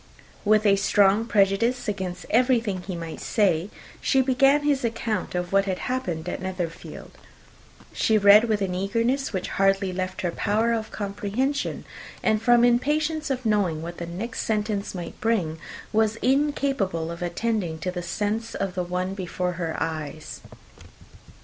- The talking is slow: No, average, 155 wpm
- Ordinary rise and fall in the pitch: Yes, average, 4.2 semitones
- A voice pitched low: No, high, 200 Hz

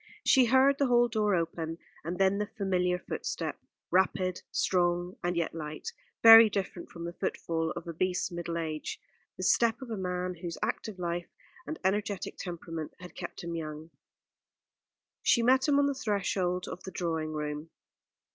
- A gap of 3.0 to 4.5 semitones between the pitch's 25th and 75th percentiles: Yes, average, 3.7 semitones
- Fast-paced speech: No, average, 165 wpm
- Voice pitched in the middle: Yes, medium, 180 Hz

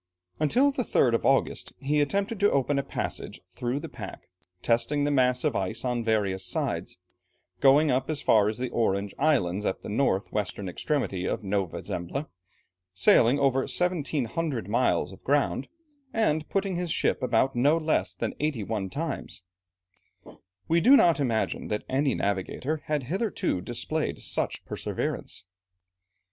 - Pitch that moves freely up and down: Yes, wide, 6.1 semitones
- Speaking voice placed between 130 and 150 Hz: Yes, low, 135 Hz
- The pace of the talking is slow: No, average, 155 wpm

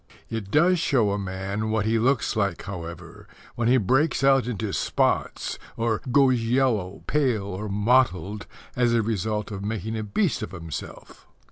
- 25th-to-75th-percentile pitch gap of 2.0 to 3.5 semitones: No, average, 3.9 semitones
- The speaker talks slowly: No, average, 160 wpm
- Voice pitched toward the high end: No, low, 110 Hz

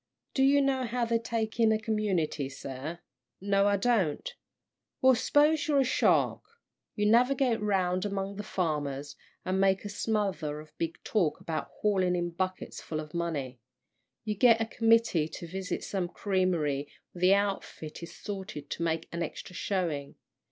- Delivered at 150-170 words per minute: Yes, average, 165 wpm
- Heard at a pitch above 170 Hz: Yes, high, 190 Hz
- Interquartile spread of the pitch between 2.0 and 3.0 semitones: No, average, 5.1 semitones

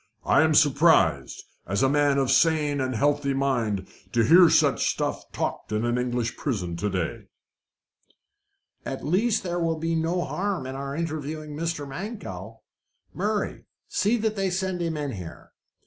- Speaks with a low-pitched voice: No, medium, 145 Hz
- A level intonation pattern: No, wide, 5.6 semitones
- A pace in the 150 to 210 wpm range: Yes, average, 160 wpm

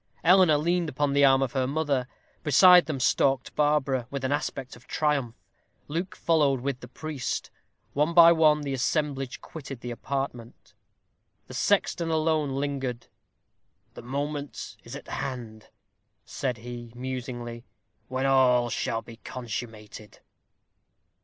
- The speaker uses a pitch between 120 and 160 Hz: Yes, low, 135 Hz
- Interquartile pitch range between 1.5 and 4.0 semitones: Yes, average, 3.4 semitones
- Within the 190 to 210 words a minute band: No, slow, 135 wpm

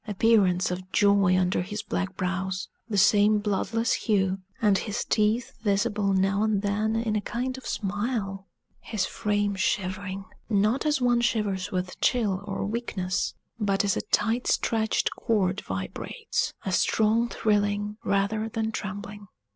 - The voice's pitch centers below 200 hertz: No, high, 205 Hz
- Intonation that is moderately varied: No, narrow, 2.3 semitones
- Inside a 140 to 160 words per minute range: Yes, average, 145 wpm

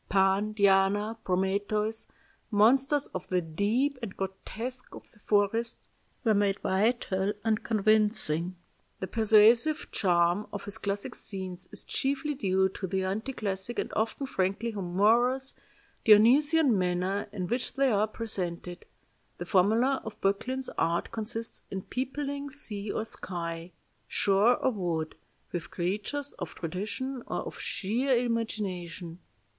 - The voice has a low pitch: No, high, 210 Hz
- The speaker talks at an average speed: No, slow, 130 wpm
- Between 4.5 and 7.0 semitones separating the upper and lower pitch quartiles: No, average, 3.8 semitones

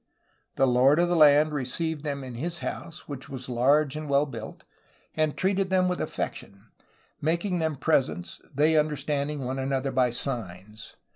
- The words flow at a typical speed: Yes, average, 165 wpm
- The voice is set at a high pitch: No, medium, 145 Hz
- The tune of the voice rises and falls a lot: No, average, 3.3 semitones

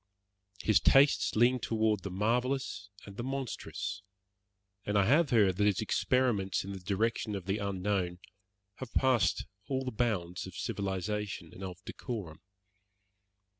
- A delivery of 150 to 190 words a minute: No, average, 140 wpm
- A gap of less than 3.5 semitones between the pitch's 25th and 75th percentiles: No, average, 4.2 semitones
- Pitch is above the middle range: No, low, 105 Hz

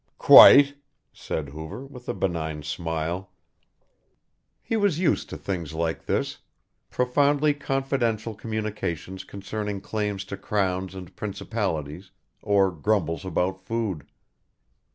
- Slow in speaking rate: Yes, slow, 110 wpm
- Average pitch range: Yes, average, 5.0 semitones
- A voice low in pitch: Yes, low, 100 Hz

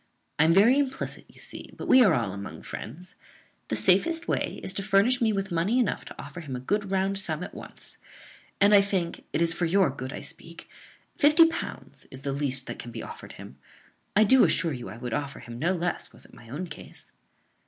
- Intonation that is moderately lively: No, wide, 6.8 semitones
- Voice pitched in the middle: Yes, medium, 175 Hz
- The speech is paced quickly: Yes, fast, 225 wpm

